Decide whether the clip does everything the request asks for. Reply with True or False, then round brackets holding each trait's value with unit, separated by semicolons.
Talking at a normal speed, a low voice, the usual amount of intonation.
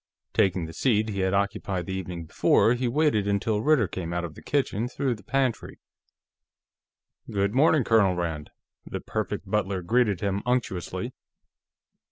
True (155 wpm; 100 Hz; 4.9 semitones)